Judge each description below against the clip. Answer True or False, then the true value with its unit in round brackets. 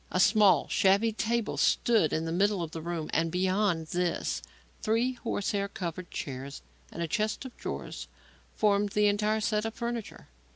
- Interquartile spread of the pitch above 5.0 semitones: False (4.1 semitones)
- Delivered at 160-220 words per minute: True (165 wpm)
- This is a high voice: True (200 Hz)